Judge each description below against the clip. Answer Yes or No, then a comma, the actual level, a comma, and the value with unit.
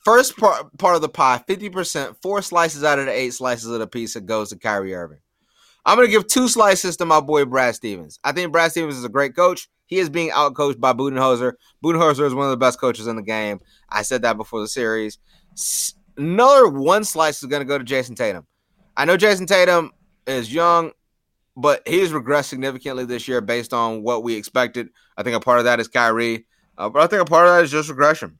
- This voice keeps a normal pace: No, fast, 230 wpm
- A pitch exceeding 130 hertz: Yes, medium, 140 Hz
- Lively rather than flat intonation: Yes, wide, 6.3 semitones